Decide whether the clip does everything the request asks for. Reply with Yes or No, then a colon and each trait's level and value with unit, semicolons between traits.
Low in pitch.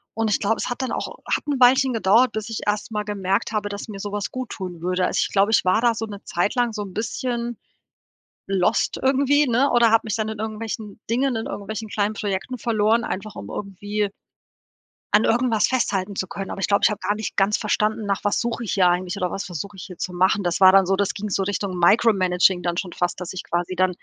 No: high, 205 Hz